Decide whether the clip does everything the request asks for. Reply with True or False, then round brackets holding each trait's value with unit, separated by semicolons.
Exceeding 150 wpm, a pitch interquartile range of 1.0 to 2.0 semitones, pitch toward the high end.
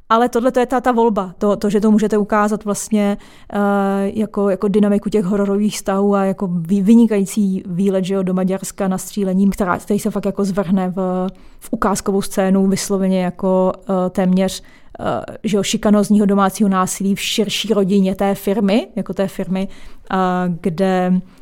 True (165 wpm; 1.6 semitones; 200 Hz)